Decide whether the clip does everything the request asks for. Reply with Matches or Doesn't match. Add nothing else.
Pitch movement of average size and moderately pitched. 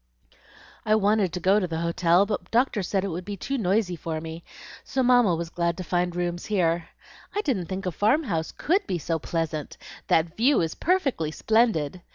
Matches